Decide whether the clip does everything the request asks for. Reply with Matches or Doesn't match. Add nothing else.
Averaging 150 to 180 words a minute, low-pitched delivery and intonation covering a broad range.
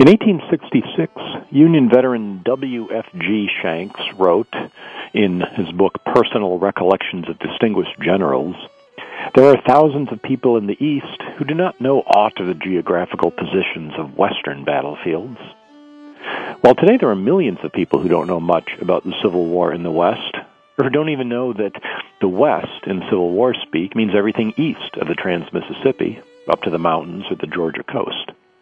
Matches